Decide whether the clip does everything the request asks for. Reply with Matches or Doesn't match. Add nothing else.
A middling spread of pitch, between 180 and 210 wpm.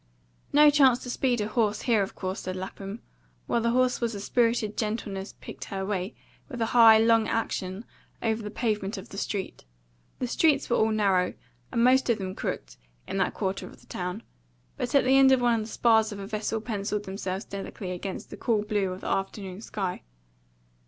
Matches